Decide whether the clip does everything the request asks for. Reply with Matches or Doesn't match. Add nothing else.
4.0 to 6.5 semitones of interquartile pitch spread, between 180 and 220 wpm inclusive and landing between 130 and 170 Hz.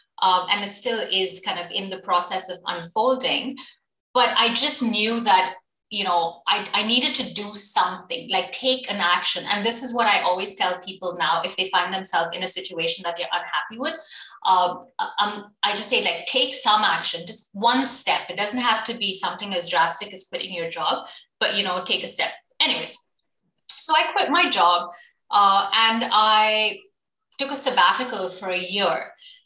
Doesn't match